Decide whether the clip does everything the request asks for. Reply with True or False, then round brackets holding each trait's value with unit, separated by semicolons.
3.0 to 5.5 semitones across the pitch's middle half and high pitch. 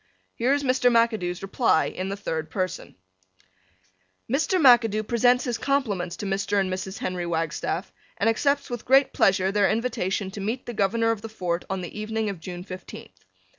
True (4.4 semitones; 210 Hz)